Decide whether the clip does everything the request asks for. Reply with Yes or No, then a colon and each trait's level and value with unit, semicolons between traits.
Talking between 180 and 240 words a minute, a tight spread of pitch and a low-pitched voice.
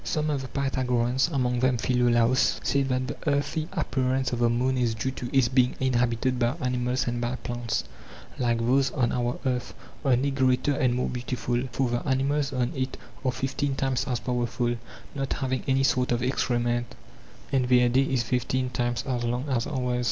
Yes: average, 185 wpm; narrow, 1.6 semitones; low, 125 Hz